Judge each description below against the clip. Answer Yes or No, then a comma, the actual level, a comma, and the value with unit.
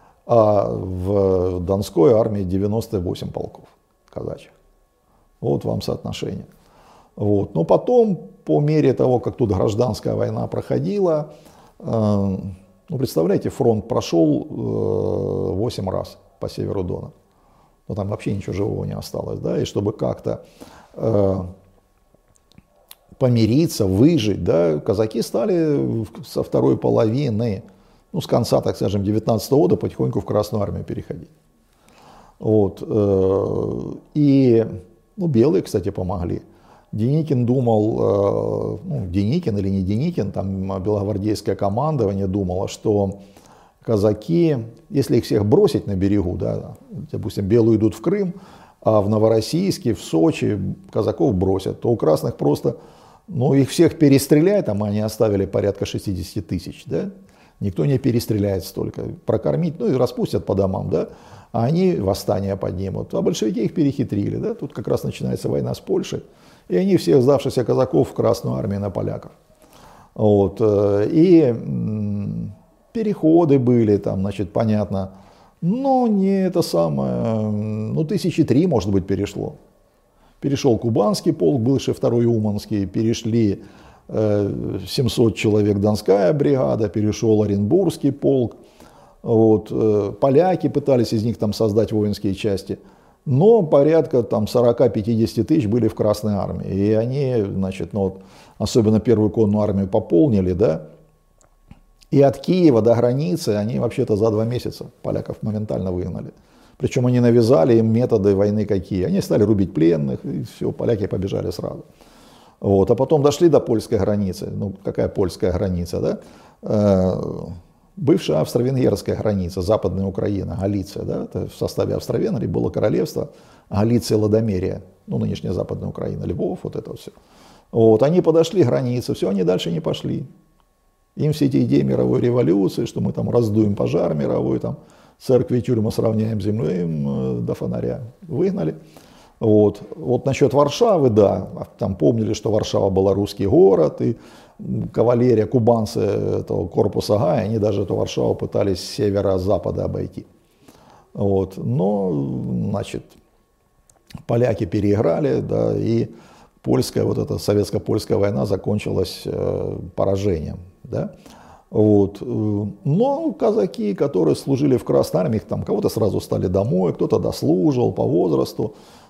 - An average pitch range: Yes, average, 4.1 semitones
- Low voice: Yes, low, 110 Hz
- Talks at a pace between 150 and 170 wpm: No, average, 130 wpm